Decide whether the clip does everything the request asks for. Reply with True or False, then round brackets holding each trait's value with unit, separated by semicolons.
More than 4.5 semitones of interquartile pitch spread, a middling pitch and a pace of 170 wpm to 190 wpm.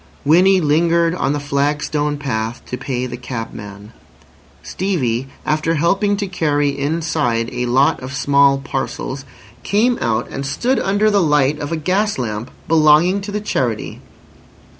False (4.9 semitones; 145 Hz; 145 wpm)